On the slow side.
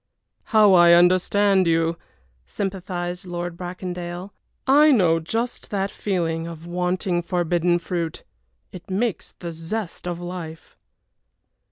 Yes: slow, 115 wpm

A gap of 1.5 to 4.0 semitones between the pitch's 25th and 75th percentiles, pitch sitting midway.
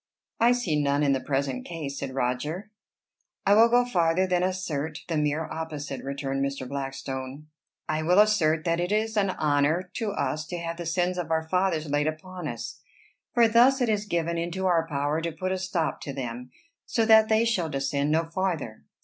No: average, 4.6 semitones; medium, 165 Hz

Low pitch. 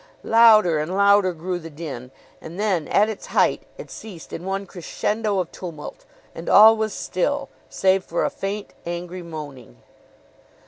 No: medium, 185 Hz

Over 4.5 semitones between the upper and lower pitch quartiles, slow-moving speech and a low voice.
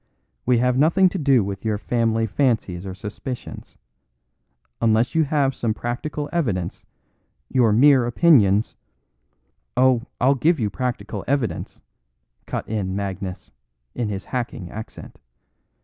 Yes: average, 4.9 semitones; slow, 130 wpm; low, 115 Hz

